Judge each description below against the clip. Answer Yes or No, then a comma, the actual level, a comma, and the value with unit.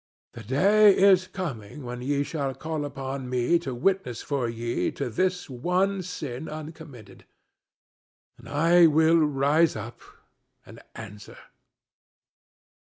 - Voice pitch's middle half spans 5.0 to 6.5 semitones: Yes, wide, 5.5 semitones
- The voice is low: No, medium, 145 Hz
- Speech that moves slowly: Yes, slow, 120 wpm